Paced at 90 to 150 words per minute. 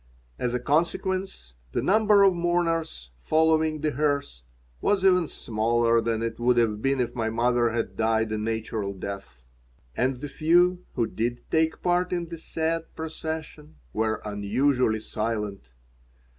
Yes: average, 145 wpm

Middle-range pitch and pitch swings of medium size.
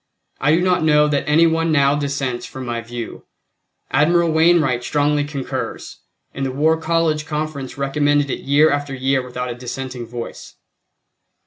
Yes: medium, 145 Hz; average, 3.0 semitones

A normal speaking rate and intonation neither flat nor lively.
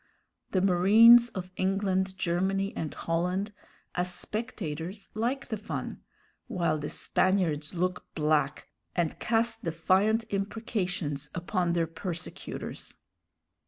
No: slow, 105 wpm; average, 3.4 semitones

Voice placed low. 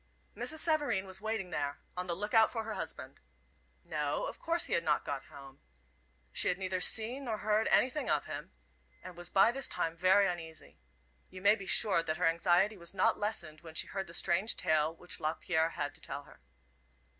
No: medium, 185 Hz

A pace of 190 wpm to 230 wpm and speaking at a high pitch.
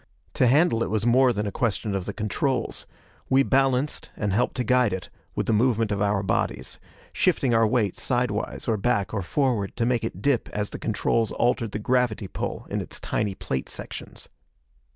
No: average, 195 wpm; low, 115 Hz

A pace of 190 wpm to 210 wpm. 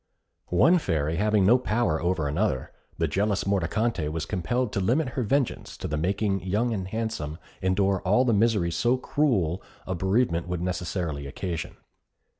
No: average, 160 wpm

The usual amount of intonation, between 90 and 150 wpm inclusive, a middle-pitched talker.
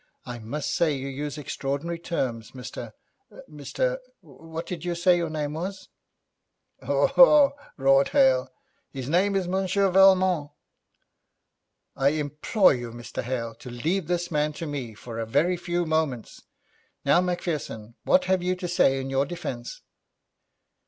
Yes: average, 5.0 semitones; average, 145 wpm; medium, 155 Hz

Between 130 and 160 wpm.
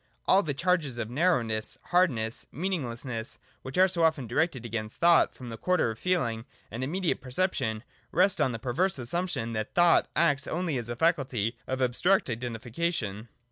No: average, 170 wpm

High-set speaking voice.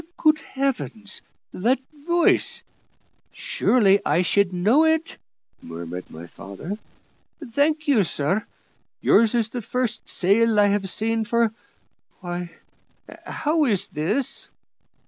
Yes: high, 220 Hz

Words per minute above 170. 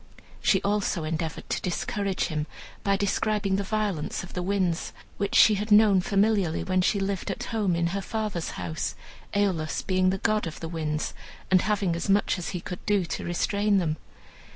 Yes: average, 185 wpm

